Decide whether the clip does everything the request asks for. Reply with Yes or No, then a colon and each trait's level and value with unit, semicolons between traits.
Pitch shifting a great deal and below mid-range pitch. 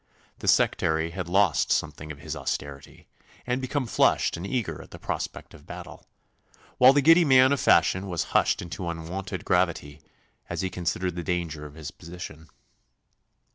No: average, 4.2 semitones; very low, 90 Hz